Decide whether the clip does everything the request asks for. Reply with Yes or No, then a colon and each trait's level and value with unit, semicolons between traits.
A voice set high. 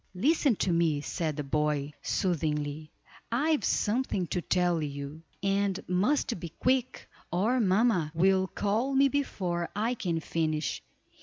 No: medium, 180 Hz